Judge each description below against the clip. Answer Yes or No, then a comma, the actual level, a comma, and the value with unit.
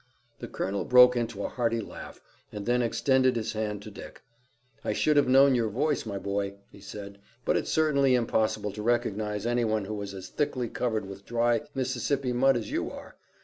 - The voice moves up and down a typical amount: Yes, average, 3.4 semitones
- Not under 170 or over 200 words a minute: Yes, average, 195 wpm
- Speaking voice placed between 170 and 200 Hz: No, low, 115 Hz